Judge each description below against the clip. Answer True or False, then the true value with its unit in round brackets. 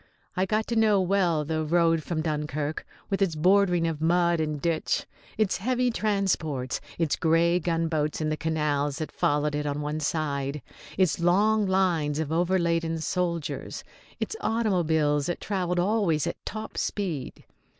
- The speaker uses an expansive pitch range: False (3.7 semitones)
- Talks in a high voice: False (165 Hz)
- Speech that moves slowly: False (155 wpm)